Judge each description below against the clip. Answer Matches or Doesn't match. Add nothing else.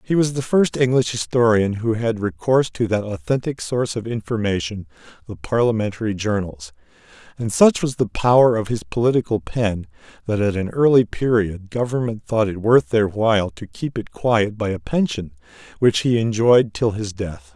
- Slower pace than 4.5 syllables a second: Doesn't match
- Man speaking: Matches